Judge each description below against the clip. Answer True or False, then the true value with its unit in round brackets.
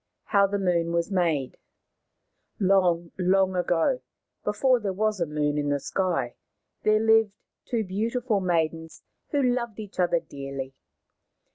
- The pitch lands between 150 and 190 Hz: True (185 Hz)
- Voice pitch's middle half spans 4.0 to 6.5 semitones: True (4.4 semitones)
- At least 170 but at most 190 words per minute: False (135 wpm)